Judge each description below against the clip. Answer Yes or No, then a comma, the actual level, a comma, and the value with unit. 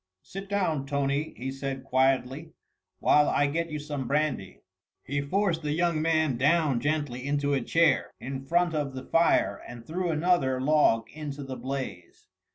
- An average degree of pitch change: Yes, average, 3.1 semitones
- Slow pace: No, average, 165 wpm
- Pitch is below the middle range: No, medium, 145 Hz